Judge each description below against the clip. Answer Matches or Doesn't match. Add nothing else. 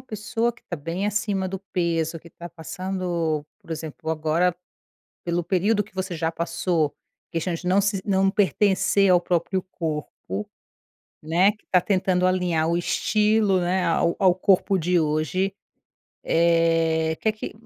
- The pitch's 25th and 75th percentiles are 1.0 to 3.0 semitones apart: Matches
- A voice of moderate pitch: Matches